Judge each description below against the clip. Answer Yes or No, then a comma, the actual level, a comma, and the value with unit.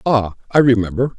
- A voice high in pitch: No, low, 115 Hz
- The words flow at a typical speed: Yes, average, 150 wpm